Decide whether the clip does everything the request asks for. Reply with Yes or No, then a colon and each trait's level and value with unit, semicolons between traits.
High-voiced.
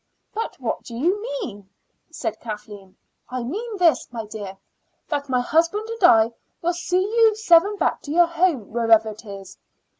Yes: very high, 295 Hz